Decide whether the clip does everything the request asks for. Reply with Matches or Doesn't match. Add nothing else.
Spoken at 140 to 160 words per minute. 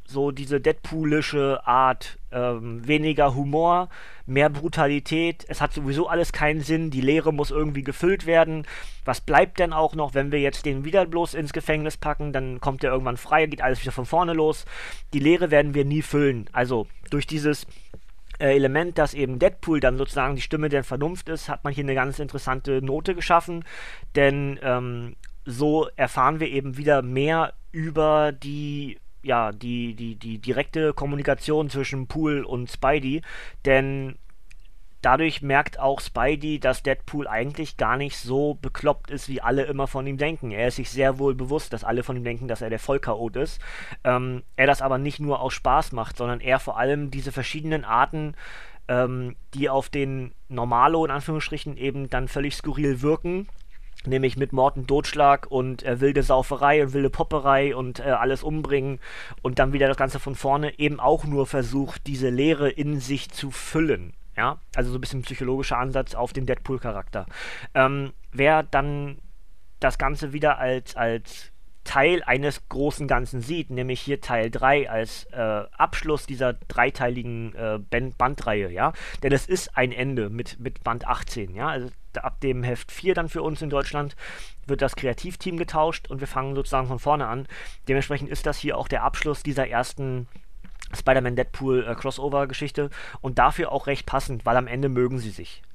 Doesn't match